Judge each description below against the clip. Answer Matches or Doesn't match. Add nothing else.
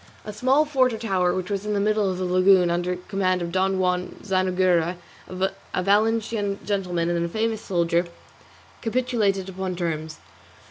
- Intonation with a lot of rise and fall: Doesn't match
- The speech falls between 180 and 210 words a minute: Doesn't match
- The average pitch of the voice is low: Doesn't match